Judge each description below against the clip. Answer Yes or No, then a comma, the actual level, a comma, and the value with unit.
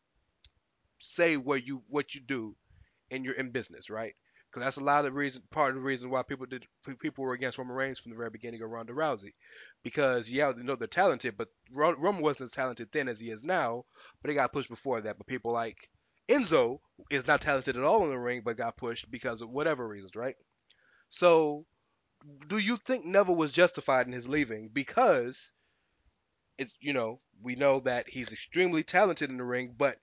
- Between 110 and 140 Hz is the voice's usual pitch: Yes, low, 135 Hz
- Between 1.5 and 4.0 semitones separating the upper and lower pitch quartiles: Yes, average, 3.2 semitones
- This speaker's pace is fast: Yes, fast, 210 wpm